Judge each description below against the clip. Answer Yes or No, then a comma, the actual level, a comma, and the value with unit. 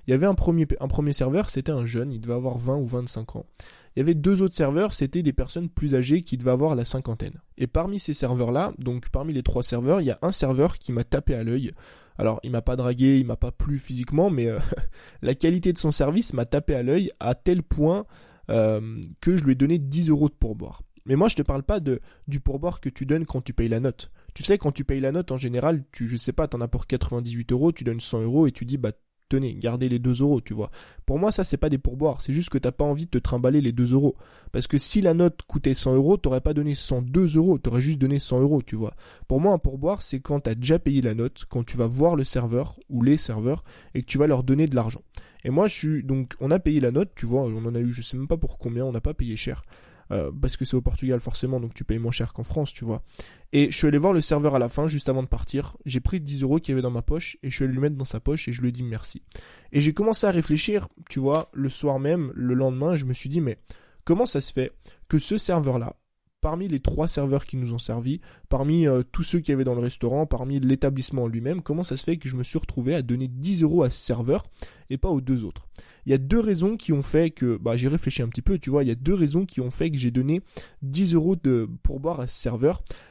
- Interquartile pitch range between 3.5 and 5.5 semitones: Yes, average, 4.0 semitones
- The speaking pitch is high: No, low, 135 Hz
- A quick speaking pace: Yes, fast, 280 wpm